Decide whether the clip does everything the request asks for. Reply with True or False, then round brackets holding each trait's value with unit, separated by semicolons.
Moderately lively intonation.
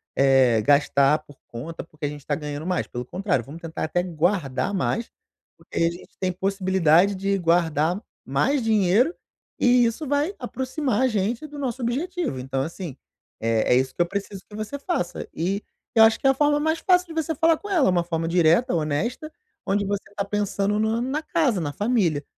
False (7.9 semitones)